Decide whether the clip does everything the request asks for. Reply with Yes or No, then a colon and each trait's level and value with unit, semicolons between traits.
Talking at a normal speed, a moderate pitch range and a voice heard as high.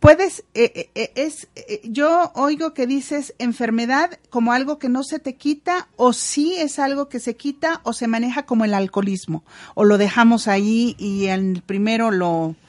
No: average, 180 wpm; wide, 5.7 semitones; high, 240 Hz